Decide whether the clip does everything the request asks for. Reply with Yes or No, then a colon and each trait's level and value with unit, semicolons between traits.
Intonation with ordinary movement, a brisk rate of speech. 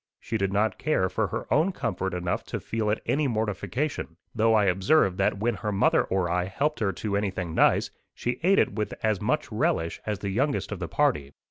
Yes: average, 4.2 semitones; fast, 215 wpm